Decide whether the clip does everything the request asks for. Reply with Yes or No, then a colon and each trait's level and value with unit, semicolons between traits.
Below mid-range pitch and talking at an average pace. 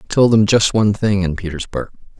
No: low, 100 Hz; fast, 220 wpm